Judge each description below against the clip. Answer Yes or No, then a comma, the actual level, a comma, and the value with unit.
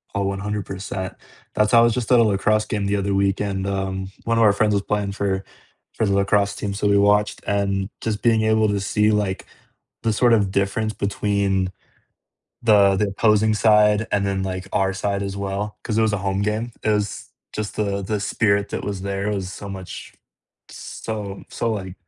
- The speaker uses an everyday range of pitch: No, narrow, 1.4 semitones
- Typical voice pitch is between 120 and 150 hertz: No, low, 100 Hz